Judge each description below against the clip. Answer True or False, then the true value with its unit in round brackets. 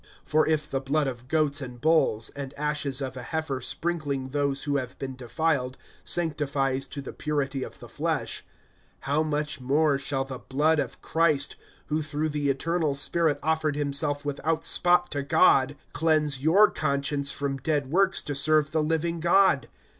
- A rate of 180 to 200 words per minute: False (170 wpm)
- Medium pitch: True (145 Hz)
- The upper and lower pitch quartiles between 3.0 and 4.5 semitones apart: False (2.4 semitones)